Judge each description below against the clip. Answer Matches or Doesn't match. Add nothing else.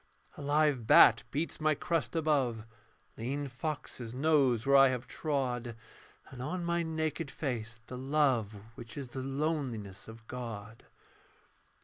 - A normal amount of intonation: Matches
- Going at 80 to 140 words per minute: Matches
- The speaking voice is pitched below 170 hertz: Matches